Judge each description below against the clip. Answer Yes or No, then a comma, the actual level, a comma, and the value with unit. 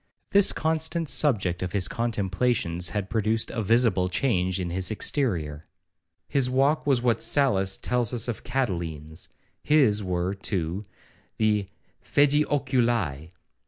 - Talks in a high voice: No, low, 105 Hz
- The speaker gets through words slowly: Yes, slow, 120 wpm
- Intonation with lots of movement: Yes, wide, 5.9 semitones